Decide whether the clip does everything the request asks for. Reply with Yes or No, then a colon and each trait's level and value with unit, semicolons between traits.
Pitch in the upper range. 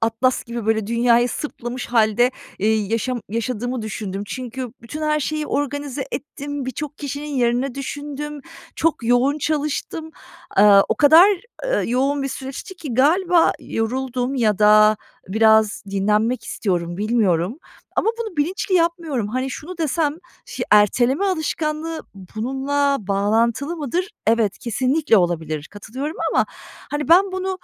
Yes: very high, 255 Hz